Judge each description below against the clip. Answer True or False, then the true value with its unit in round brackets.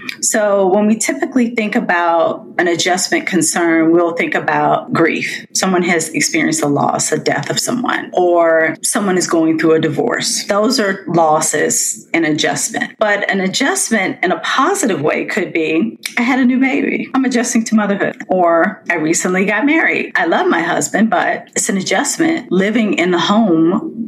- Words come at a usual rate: True (170 wpm)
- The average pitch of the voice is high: True (195 Hz)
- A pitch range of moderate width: False (5.7 semitones)